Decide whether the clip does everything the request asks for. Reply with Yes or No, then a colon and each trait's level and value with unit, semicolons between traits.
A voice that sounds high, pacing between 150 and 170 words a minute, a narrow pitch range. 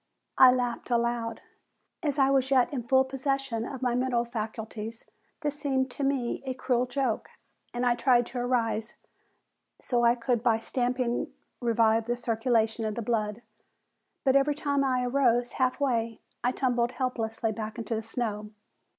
Yes: high, 245 Hz; average, 160 wpm; narrow, 2.3 semitones